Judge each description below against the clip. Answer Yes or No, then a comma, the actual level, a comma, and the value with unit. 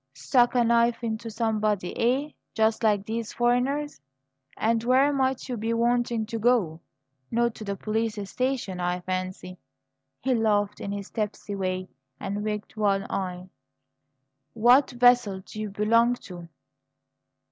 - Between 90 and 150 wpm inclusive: Yes, average, 140 wpm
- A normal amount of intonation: Yes, average, 3.2 semitones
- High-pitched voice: Yes, high, 220 Hz